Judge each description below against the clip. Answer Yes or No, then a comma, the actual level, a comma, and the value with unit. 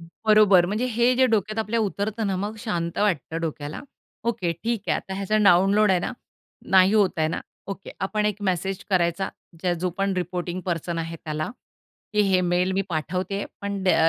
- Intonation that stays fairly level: No, average, 3.3 semitones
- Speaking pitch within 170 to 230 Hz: Yes, high, 190 Hz